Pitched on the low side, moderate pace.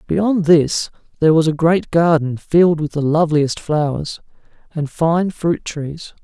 No: medium, 160 Hz; average, 155 wpm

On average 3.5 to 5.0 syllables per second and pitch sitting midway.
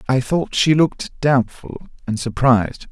No: 4.5 syllables/s; low, 130 Hz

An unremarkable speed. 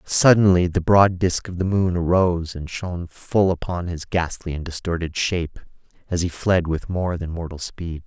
Yes: average, 185 wpm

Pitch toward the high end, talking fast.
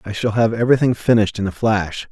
No: low, 110 Hz; fast, 225 wpm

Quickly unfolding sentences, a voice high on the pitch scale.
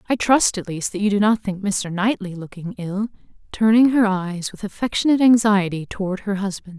No: average, 195 wpm; high, 200 Hz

